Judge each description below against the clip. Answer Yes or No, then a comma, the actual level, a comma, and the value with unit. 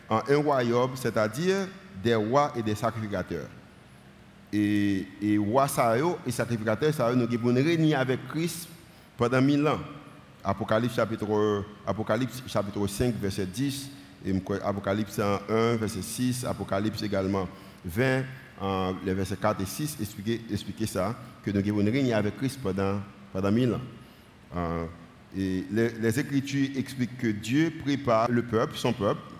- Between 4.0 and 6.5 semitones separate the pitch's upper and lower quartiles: Yes, average, 4.6 semitones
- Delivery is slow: Yes, slow, 135 wpm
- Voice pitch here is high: No, low, 110 Hz